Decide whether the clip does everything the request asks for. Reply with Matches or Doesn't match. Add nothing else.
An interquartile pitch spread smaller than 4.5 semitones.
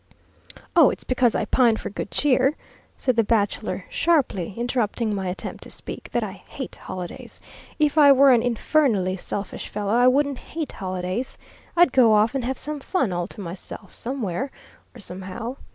Doesn't match